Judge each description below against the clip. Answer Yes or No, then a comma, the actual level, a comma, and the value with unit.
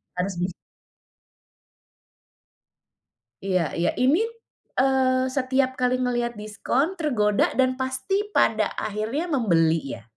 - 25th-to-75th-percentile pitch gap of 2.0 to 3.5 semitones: No, average, 4.3 semitones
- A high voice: Yes, very high, 255 Hz